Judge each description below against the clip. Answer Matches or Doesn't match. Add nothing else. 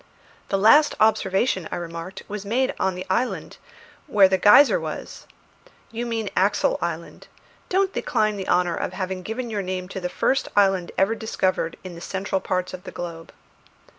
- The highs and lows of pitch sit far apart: Doesn't match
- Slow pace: Doesn't match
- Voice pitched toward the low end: Doesn't match